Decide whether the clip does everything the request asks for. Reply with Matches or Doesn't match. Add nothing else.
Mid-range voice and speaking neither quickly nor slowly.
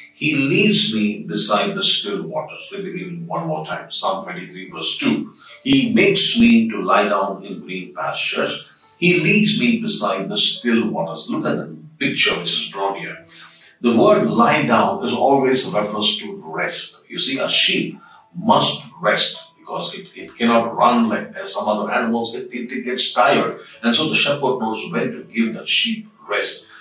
Matches